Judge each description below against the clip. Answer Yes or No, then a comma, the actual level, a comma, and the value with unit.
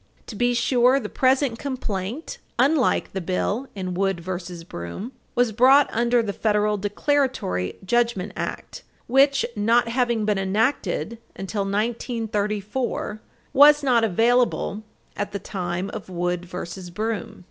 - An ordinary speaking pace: No, slow, 130 wpm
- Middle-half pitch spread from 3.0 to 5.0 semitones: Yes, average, 4.1 semitones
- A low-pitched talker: No, high, 215 Hz